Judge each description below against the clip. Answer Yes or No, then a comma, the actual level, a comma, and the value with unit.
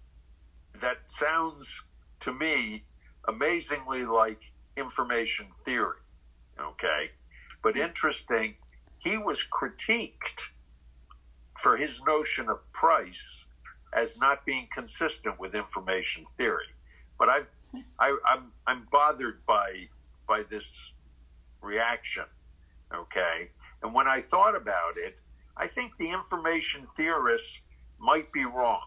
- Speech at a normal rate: No, slow, 105 wpm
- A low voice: Yes, very low, 75 Hz